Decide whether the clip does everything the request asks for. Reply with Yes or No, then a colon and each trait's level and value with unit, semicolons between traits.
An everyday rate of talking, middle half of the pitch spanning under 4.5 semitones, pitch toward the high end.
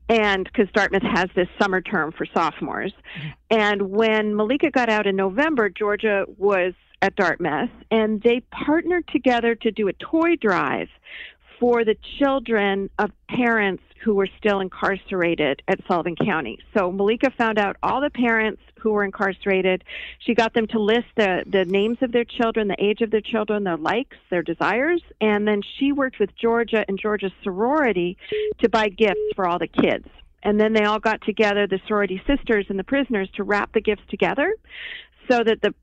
Yes: average, 180 wpm; average, 3.1 semitones; high, 215 Hz